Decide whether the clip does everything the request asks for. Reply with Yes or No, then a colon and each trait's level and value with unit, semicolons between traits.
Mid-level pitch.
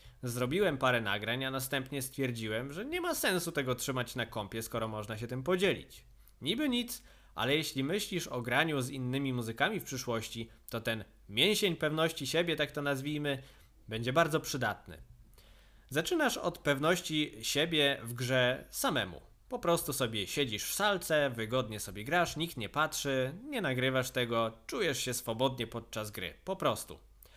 No: low, 130 Hz